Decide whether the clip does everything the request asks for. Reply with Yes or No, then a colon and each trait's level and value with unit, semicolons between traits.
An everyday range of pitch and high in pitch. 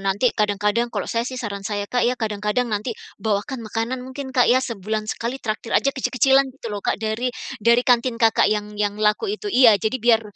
Yes: average, 3.1 semitones; high, 230 Hz